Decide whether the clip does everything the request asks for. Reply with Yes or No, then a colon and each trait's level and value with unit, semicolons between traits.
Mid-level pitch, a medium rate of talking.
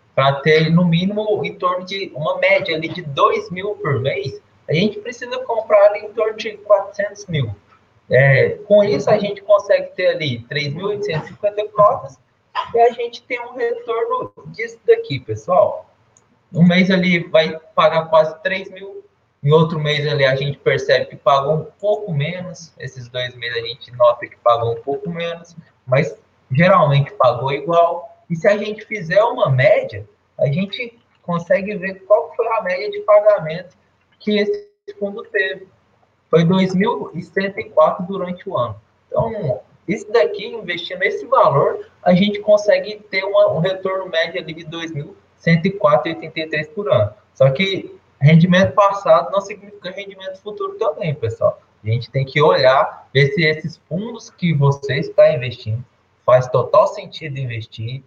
Yes: medium, 180 Hz; average, 155 wpm